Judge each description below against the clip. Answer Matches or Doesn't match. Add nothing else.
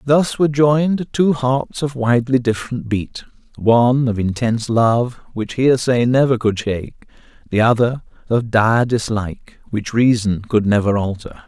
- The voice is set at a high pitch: Doesn't match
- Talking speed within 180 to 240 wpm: Doesn't match